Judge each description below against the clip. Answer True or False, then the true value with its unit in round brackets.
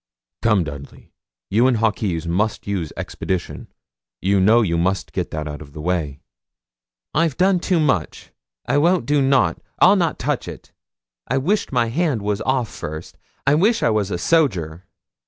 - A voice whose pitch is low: True (105 Hz)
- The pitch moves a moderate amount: False (8.2 semitones)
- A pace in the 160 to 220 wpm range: True (170 wpm)